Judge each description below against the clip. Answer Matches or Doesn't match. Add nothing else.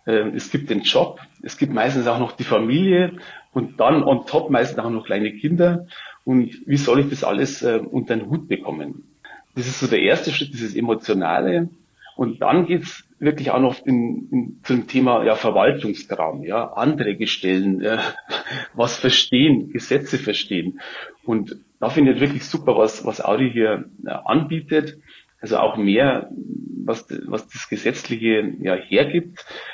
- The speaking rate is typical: Matches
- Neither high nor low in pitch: Doesn't match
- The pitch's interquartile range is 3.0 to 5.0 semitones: Doesn't match